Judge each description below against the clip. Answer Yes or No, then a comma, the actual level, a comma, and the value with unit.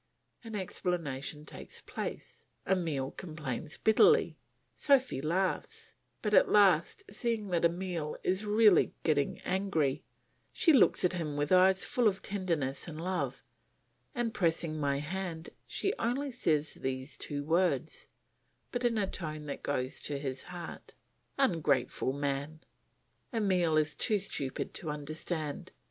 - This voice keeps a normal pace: No, slow, 130 wpm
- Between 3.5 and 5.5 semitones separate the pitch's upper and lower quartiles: Yes, average, 5.2 semitones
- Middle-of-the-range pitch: Yes, medium, 170 Hz